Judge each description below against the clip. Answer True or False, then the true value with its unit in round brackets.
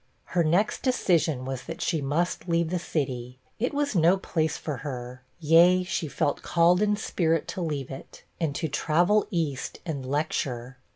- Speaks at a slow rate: False (170 wpm)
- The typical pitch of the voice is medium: True (160 Hz)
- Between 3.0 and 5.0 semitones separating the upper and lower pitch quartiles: True (4.5 semitones)